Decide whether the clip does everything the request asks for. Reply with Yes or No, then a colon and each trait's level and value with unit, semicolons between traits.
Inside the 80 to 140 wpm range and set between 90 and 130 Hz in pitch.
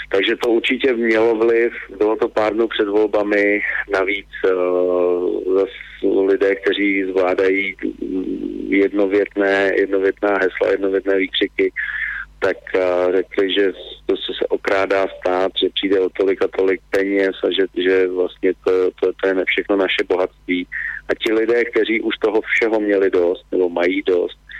No: average, 150 wpm; low, 110 Hz